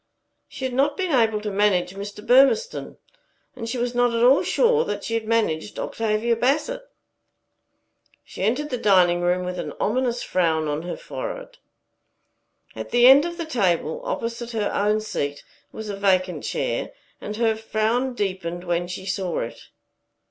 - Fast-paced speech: No, average, 165 wpm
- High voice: Yes, high, 220 Hz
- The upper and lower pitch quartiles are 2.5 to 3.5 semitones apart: No, average, 5.3 semitones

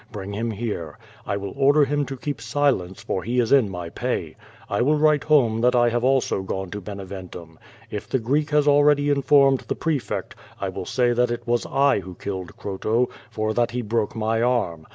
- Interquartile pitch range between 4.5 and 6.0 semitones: Yes, wide, 5.5 semitones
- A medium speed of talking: No, fast, 210 wpm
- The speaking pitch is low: Yes, low, 120 Hz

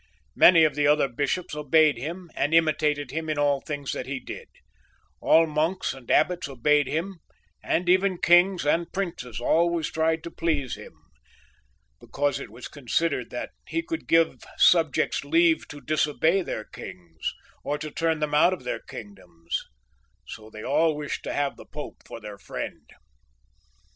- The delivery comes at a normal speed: Yes, average, 160 wpm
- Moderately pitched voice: Yes, medium, 150 Hz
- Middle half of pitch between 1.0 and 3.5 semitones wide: Yes, average, 3.0 semitones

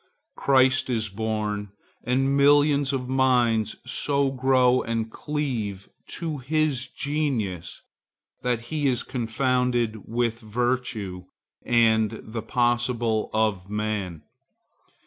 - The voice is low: Yes, low, 120 Hz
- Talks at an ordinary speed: No, slow, 100 wpm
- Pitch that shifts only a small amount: No, average, 3.3 semitones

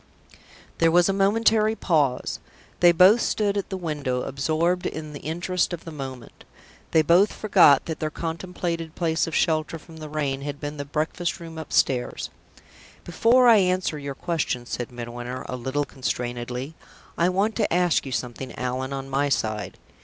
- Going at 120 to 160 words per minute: No, average, 170 wpm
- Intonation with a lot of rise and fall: No, average, 4.8 semitones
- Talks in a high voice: No, medium, 155 Hz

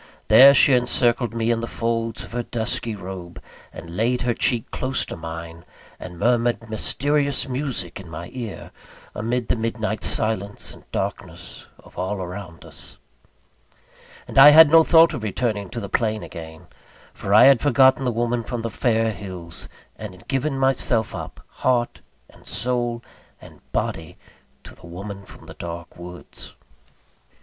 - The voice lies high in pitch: No, low, 115 Hz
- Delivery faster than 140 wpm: Yes, average, 160 wpm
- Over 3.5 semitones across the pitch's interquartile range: Yes, average, 4.8 semitones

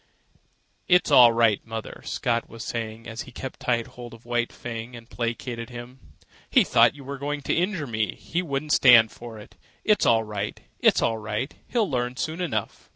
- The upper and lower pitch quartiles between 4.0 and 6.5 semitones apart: No, average, 3.4 semitones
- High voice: No, low, 120 Hz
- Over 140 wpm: Yes, average, 195 wpm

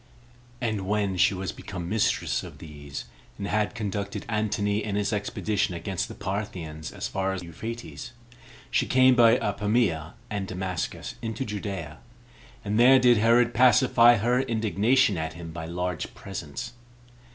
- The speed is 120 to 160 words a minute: Yes, average, 145 wpm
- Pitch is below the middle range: Yes, low, 105 Hz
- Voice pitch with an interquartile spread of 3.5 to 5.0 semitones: Yes, average, 4.3 semitones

